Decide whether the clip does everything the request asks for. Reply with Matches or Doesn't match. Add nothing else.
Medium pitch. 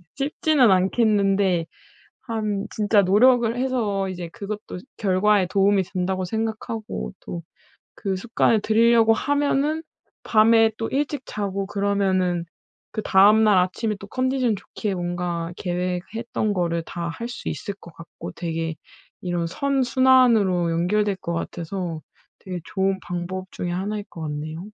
Doesn't match